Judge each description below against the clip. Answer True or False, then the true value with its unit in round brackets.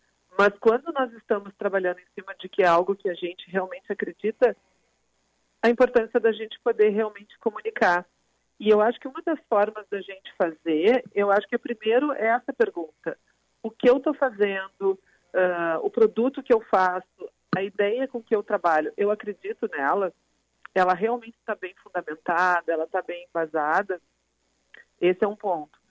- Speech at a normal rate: True (175 wpm)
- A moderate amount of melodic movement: True (4.0 semitones)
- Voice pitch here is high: True (205 Hz)